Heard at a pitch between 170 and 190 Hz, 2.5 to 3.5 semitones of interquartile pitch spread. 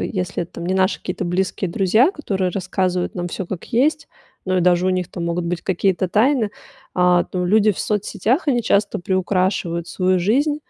Yes: medium, 185 Hz; average, 2.9 semitones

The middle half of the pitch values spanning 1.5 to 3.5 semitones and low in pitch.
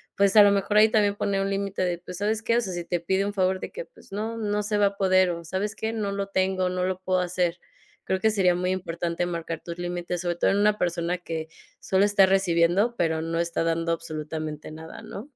No: average, 2.9 semitones; medium, 185 Hz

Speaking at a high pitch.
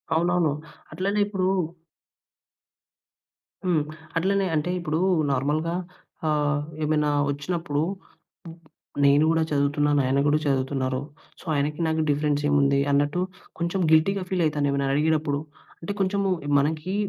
No: medium, 150 Hz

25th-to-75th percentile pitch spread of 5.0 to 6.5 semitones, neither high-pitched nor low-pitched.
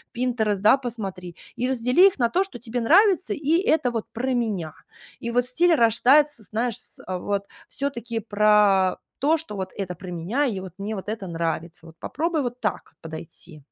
No: wide, 5.4 semitones; high, 230 Hz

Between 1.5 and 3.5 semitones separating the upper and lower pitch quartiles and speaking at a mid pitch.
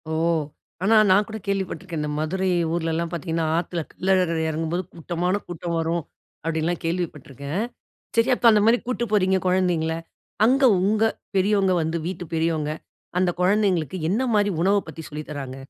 Yes: average, 3.0 semitones; medium, 175 Hz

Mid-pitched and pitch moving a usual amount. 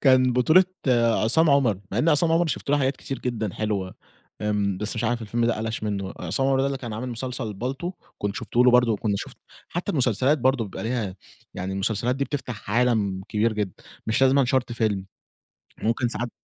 No: low, 120 Hz; average, 3.7 semitones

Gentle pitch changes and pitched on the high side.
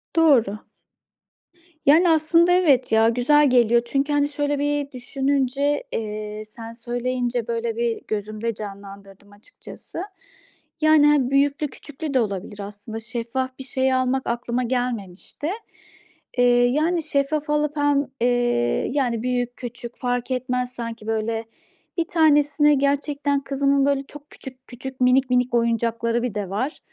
No: average, 3.7 semitones; very high, 250 Hz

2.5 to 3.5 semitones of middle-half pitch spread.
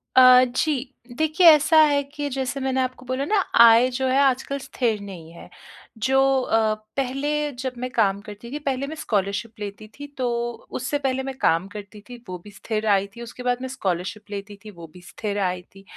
No: average, 4.6 semitones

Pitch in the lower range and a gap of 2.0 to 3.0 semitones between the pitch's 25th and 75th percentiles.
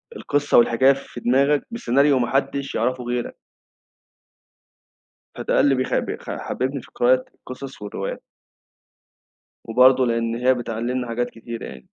Yes: low, 125 Hz; narrow, 2.4 semitones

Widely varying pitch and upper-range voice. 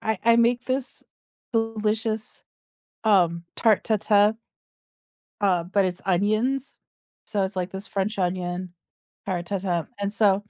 No: average, 3.1 semitones; high, 205 Hz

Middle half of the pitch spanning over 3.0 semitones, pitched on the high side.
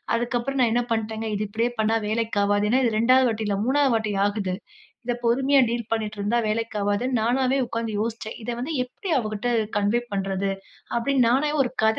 No: average, 2.7 semitones; high, 230 Hz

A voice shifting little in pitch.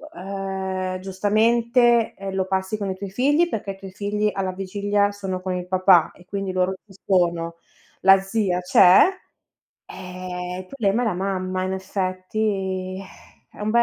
Yes: narrow, 1.6 semitones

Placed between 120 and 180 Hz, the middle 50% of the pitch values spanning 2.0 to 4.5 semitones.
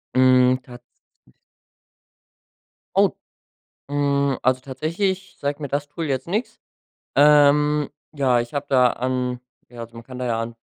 Yes: low, 135 Hz; narrow, 2.6 semitones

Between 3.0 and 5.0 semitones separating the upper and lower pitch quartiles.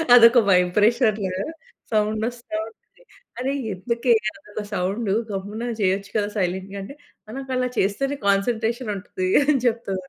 Yes: average, 3.5 semitones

